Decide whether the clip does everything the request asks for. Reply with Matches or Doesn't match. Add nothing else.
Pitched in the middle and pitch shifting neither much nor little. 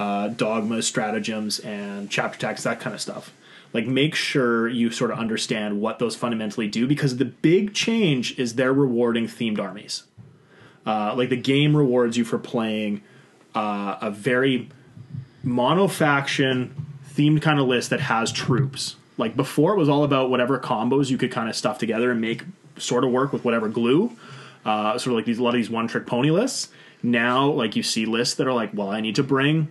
Doesn't match